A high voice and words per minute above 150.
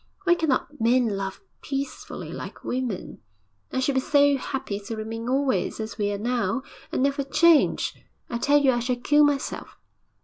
Yes: very high, 255 Hz; average, 170 wpm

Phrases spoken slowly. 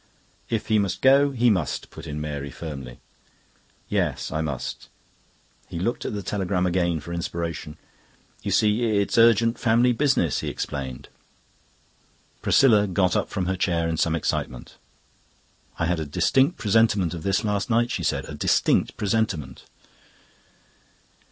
No: average, 145 wpm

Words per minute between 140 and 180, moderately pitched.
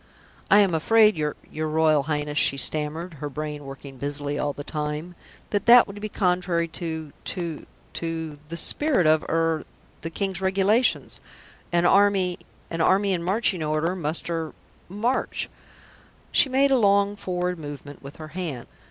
Yes: average, 160 wpm; medium, 165 Hz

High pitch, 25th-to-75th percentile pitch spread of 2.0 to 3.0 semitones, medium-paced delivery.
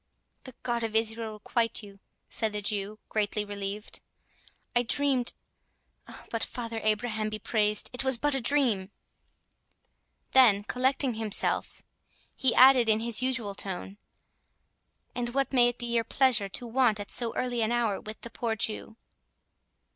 Yes: high, 230 Hz; narrow, 2.6 semitones; average, 145 wpm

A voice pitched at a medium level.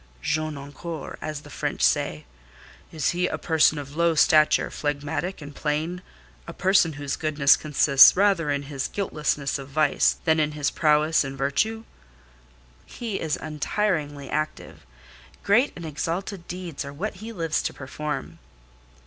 Yes: medium, 155 Hz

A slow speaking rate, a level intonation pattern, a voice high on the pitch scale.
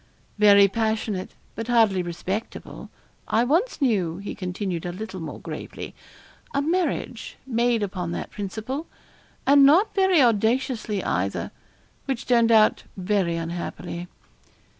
No: slow, 120 wpm; average, 5.1 semitones; high, 215 Hz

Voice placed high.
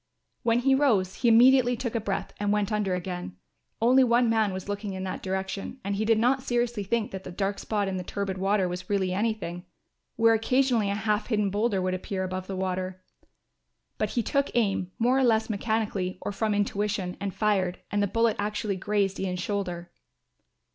Yes: high, 205 Hz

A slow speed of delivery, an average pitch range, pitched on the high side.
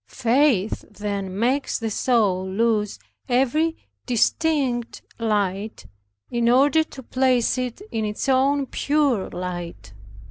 Yes: slow, 110 wpm; average, 4.4 semitones; high, 235 Hz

